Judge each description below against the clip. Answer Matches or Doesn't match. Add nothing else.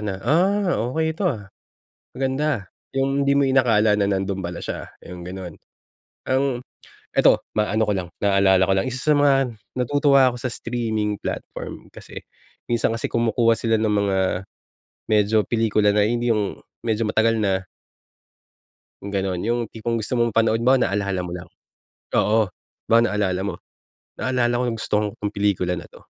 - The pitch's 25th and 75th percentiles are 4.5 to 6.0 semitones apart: Doesn't match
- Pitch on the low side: Matches